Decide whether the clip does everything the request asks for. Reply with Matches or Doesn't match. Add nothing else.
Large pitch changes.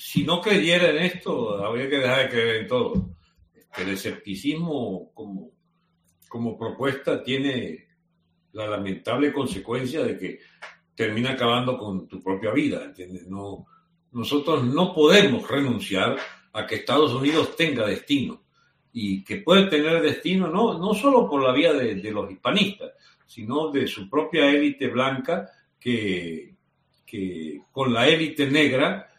Matches